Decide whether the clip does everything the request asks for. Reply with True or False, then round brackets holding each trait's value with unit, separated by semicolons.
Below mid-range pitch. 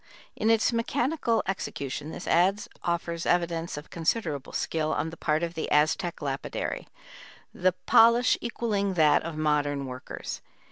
False (170 Hz)